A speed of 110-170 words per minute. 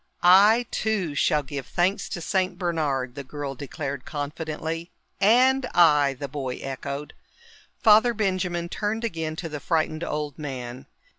Yes: average, 140 wpm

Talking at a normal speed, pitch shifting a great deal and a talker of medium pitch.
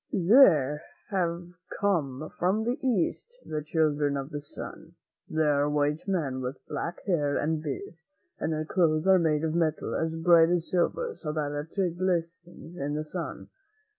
No: average, 165 wpm; average, 3.0 semitones; medium, 160 Hz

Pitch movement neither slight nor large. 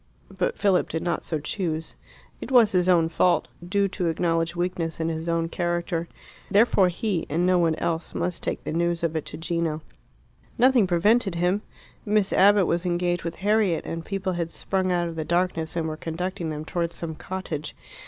No: narrow, 2.2 semitones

